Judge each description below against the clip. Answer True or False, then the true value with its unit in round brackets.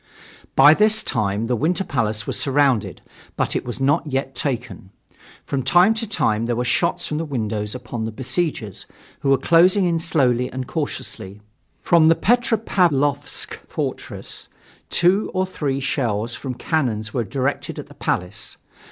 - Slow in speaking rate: False (155 wpm)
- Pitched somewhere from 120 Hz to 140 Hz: True (135 Hz)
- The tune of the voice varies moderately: False (6.2 semitones)